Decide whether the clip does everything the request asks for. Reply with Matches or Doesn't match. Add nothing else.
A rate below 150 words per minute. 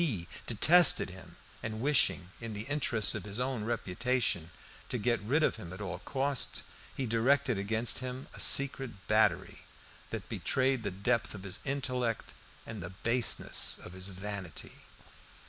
Doesn't match